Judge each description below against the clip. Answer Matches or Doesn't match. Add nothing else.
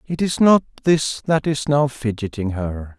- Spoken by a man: Matches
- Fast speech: Doesn't match